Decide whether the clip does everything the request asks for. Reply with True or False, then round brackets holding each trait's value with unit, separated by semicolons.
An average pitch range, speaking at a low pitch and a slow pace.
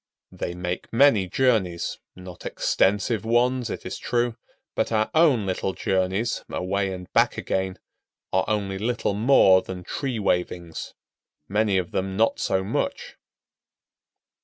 True (3.7 semitones; 100 Hz; 130 wpm)